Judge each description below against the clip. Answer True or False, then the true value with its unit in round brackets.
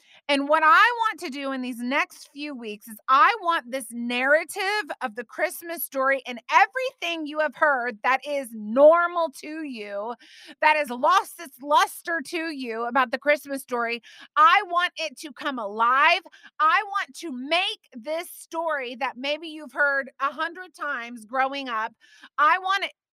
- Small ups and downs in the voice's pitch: False (4.3 semitones)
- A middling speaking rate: True (170 wpm)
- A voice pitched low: False (295 Hz)